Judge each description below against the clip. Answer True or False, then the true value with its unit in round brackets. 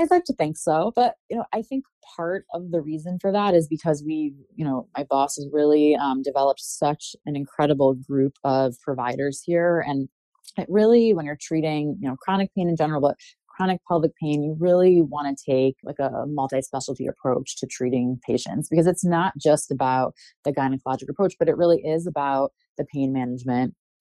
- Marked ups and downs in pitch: False (4.3 semitones)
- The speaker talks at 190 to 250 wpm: True (195 wpm)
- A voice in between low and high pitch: True (150 Hz)